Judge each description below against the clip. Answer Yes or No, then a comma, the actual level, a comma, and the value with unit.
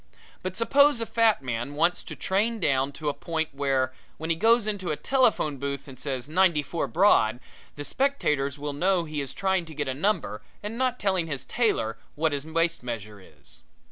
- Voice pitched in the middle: Yes, medium, 160 Hz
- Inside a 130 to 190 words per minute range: No, average, 200 wpm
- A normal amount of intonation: No, wide, 6.0 semitones